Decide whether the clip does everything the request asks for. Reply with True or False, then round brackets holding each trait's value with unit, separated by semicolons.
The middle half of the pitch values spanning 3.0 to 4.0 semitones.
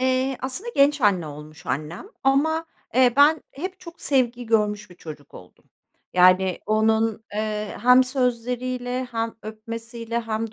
True (3.5 semitones)